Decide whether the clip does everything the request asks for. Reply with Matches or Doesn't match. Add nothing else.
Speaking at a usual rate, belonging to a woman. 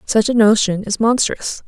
Matches